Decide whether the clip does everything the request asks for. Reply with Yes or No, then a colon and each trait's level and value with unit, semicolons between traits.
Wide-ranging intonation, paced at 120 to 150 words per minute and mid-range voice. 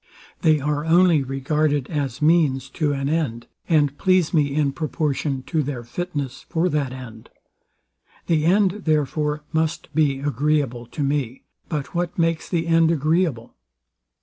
No: average, 2.9 semitones; average, 145 wpm; medium, 150 Hz